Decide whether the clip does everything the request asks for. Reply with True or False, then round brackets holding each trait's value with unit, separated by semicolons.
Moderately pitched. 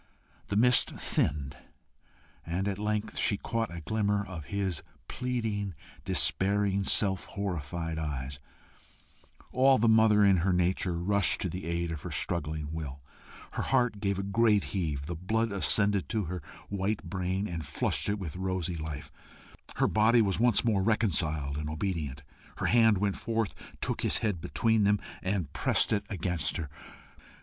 False (95 Hz)